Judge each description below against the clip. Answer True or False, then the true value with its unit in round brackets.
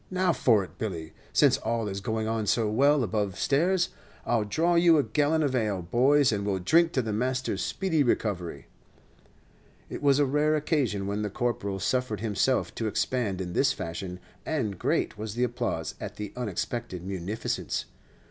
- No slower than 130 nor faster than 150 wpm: False (175 wpm)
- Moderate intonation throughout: False (5.8 semitones)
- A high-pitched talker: False (115 Hz)